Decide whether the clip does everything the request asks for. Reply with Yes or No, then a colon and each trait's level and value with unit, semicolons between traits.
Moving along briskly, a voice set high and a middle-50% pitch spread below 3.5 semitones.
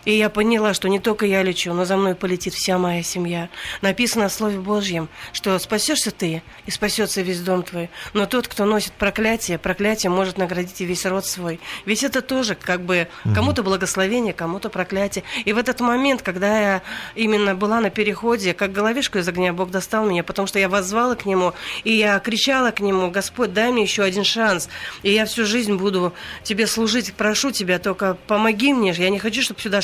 Yes: fast, 200 wpm; high, 200 Hz; average, 2.9 semitones